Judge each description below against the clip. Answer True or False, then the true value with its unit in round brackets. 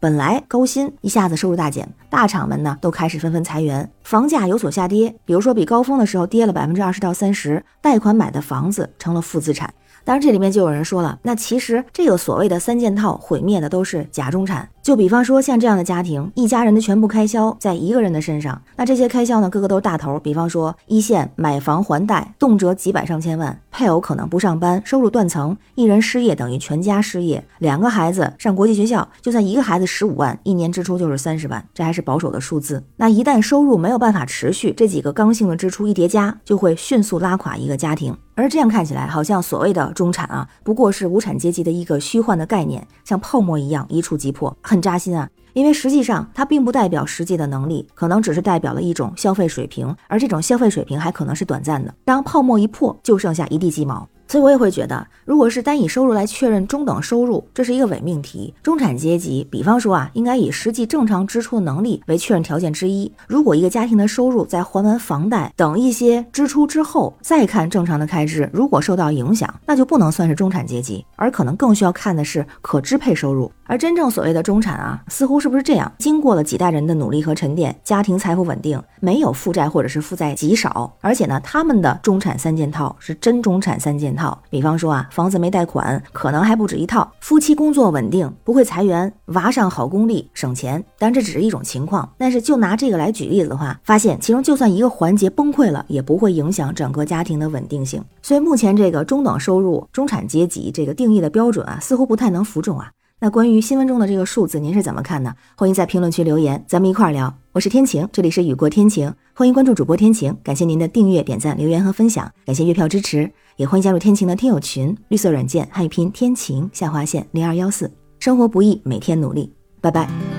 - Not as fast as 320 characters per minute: False (355 characters per minute)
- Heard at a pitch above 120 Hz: True (185 Hz)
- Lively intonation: True (6.1 semitones)